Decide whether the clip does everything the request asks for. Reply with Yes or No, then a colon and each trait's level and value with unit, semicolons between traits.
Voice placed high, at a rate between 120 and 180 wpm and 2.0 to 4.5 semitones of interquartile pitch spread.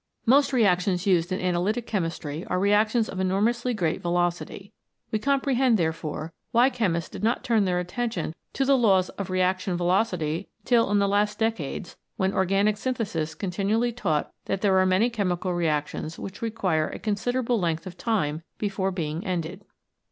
Yes: high, 195 Hz; average, 160 wpm; average, 4.2 semitones